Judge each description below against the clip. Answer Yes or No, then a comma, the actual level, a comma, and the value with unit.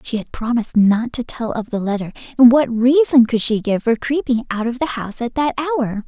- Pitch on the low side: No, high, 240 Hz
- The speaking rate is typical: No, fast, 235 wpm